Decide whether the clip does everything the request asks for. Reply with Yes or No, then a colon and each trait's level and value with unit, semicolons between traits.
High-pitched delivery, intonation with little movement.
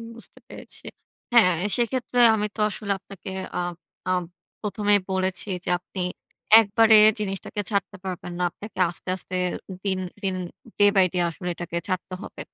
Yes: high, 195 Hz; narrow, 2.3 semitones